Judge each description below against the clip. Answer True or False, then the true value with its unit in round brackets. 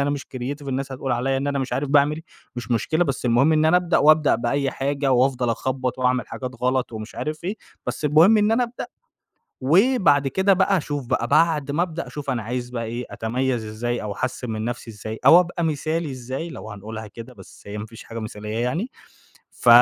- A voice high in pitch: False (135 Hz)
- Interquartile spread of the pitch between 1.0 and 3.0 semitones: False (4.4 semitones)